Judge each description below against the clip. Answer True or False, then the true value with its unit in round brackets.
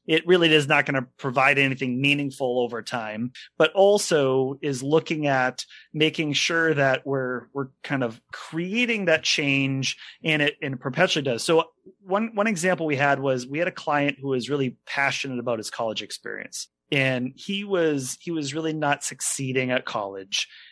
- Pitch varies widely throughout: False (3.5 semitones)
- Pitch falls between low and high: True (145 Hz)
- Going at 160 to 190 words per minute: True (175 wpm)